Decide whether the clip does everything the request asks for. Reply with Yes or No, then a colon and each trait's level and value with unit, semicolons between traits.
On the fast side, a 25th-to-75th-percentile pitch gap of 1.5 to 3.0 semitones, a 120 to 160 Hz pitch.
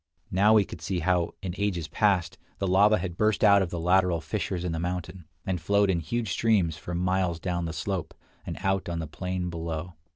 No: fast, 215 wpm; narrow, 2.4 semitones; very low, 90 Hz